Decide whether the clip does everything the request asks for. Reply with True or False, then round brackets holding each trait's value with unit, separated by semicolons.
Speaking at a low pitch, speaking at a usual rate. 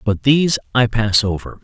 True (115 Hz; 185 wpm)